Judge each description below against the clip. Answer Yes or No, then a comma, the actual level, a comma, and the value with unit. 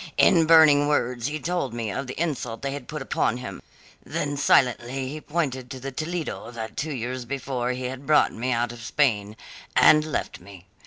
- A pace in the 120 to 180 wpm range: No, average, 195 wpm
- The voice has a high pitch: No, low, 130 Hz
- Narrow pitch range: No, average, 3.5 semitones